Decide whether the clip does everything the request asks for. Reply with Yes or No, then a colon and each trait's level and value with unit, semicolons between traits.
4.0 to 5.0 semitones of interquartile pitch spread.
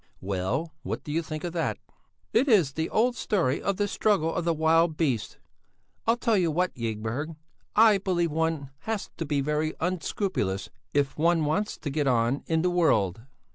Yes: average, 4.5 semitones